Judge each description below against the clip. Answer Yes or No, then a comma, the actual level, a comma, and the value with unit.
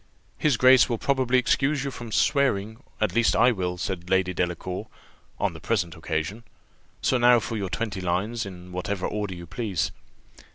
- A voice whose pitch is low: Yes, low, 105 Hz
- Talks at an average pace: Yes, average, 170 wpm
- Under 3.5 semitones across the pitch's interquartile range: No, average, 5.0 semitones